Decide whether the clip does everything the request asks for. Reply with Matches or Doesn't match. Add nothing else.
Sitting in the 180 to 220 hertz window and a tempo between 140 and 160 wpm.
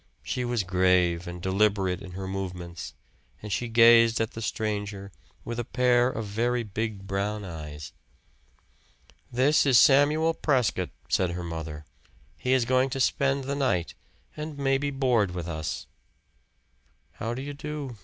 Doesn't match